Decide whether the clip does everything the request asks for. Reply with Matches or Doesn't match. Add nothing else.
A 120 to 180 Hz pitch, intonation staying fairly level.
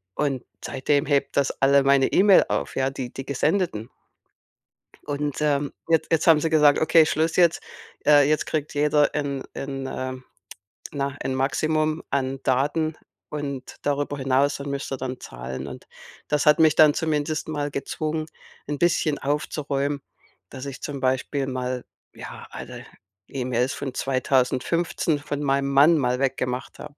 Matches